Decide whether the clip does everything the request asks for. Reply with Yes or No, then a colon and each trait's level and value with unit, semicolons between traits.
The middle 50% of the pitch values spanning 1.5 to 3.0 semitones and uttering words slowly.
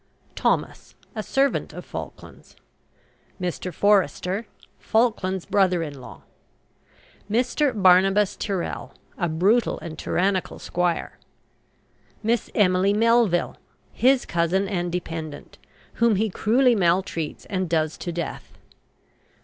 No: average, 3.8 semitones; slow, 105 wpm